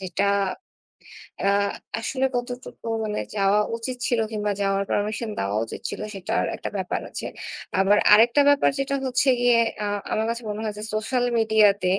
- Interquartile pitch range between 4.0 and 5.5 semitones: No, average, 3.2 semitones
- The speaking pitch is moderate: No, high, 215 Hz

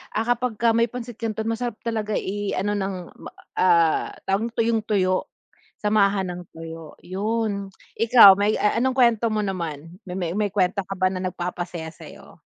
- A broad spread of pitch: No, average, 3.4 semitones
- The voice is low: No, high, 205 Hz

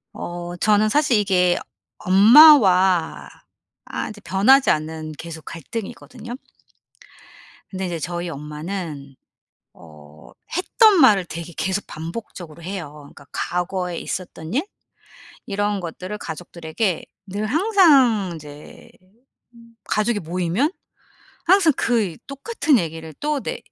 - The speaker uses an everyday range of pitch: No, wide, 5.8 semitones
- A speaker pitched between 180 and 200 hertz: Yes, medium, 185 Hz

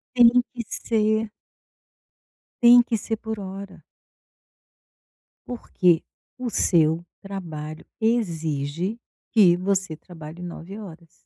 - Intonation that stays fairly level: No, average, 5.1 semitones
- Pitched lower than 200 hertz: Yes, high, 190 Hz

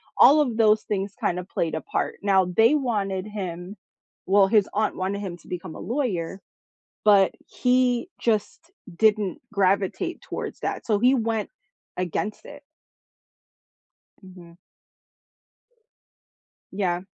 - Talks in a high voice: Yes, high, 200 Hz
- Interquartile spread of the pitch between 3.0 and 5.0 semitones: Yes, average, 3.4 semitones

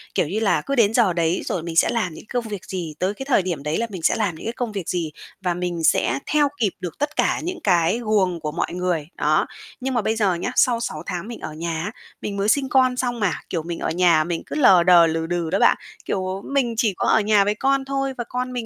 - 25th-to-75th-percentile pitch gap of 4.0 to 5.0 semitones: No, wide, 5.6 semitones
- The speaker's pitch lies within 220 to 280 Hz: No, high, 195 Hz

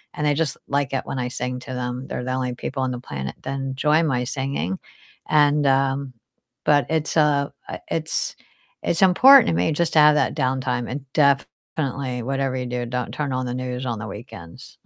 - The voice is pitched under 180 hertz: Yes, low, 135 Hz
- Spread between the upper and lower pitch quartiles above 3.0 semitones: No, average, 2.7 semitones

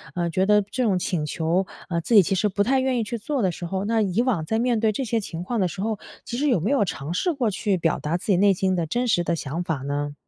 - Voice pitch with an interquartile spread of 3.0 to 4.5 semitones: No, average, 5.1 semitones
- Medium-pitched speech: No, high, 195 Hz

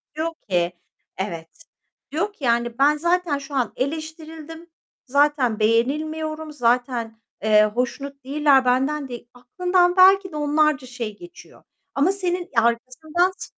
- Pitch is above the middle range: Yes, very high, 285 Hz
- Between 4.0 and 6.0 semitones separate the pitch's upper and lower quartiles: Yes, average, 4.7 semitones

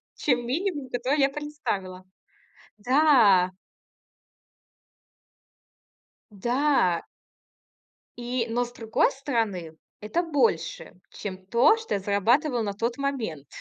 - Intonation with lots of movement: Yes, wide, 5.7 semitones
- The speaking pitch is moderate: No, high, 240 Hz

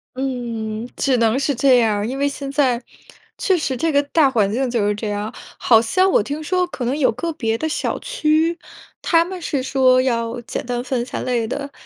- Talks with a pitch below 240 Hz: No, very high, 260 Hz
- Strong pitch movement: No, average, 4.3 semitones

